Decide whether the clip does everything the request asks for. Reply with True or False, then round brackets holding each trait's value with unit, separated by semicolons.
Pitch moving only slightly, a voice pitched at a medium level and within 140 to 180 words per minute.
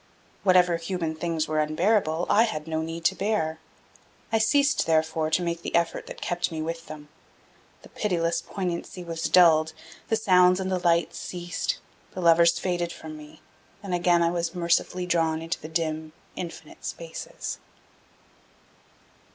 True (2.1 semitones; 170 Hz; 155 wpm)